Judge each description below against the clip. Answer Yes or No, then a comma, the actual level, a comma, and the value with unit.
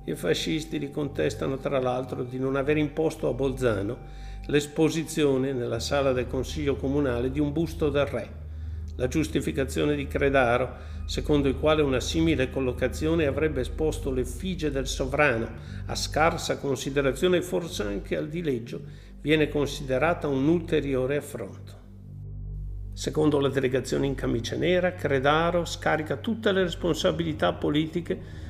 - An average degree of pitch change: Yes, average, 4.1 semitones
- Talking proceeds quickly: No, average, 135 wpm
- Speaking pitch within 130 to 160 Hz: Yes, low, 135 Hz